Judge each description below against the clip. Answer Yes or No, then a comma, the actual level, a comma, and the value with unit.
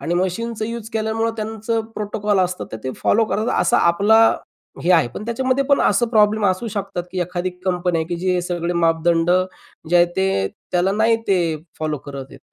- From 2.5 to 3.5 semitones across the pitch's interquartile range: No, average, 4.1 semitones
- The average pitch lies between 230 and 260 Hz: No, high, 190 Hz